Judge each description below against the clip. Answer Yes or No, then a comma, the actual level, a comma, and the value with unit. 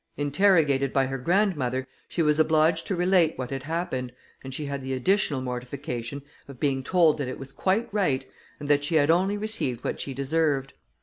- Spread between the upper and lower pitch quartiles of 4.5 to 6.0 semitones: No, average, 4.0 semitones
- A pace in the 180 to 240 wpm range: Yes, average, 190 wpm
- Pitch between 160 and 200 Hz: No, medium, 145 Hz